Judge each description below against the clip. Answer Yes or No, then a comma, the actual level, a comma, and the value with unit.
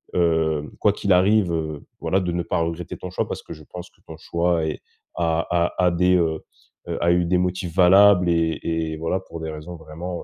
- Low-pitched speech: Yes, very low, 85 Hz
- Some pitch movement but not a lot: No, narrow, 1.9 semitones